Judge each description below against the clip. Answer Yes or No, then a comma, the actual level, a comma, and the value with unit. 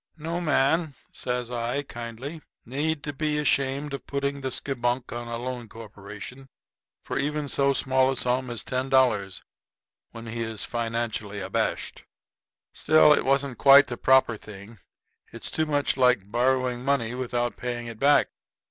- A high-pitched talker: No, low, 130 Hz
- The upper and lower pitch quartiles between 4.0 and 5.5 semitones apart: No, average, 2.9 semitones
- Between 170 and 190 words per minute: No, average, 155 wpm